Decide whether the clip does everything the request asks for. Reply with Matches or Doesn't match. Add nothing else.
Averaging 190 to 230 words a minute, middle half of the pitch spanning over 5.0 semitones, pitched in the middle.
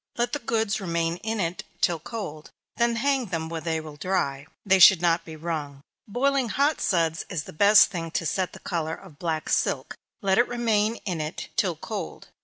Matches